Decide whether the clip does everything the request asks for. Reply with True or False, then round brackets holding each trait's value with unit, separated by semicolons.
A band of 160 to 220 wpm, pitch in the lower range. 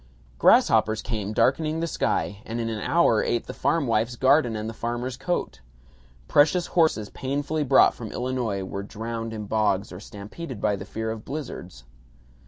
True (165 wpm; 115 Hz)